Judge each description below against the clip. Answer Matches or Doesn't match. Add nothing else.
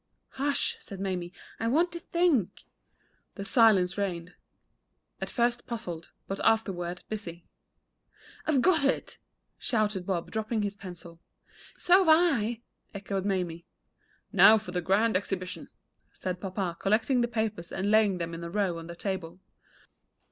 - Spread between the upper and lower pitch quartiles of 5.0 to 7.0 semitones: Doesn't match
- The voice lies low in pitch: Doesn't match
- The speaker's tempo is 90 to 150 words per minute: Matches